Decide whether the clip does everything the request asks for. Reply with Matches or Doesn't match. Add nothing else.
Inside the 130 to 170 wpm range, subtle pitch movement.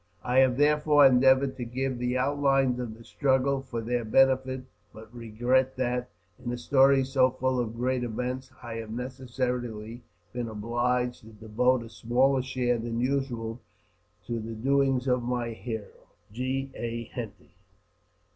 Matches